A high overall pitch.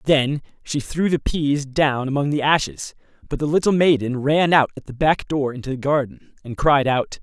No: medium, 140 Hz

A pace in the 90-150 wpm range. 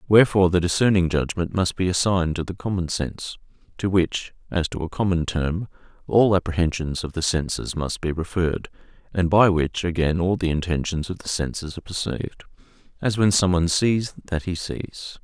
No: average, 175 wpm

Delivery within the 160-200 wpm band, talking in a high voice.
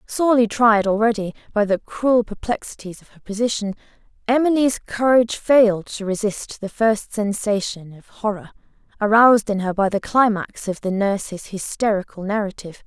No: average, 145 wpm; high, 215 Hz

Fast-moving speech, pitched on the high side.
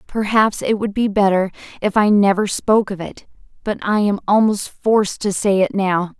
No: average, 195 wpm; high, 200 Hz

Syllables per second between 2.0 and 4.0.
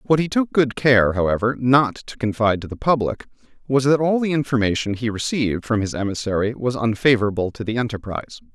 No: 5.9 syllables/s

